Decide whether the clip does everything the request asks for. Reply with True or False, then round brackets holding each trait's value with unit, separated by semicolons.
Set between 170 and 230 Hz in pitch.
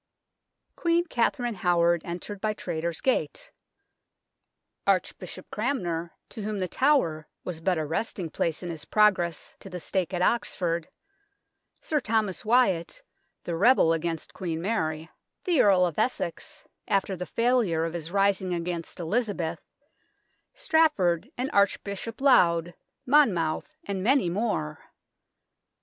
True (185 Hz)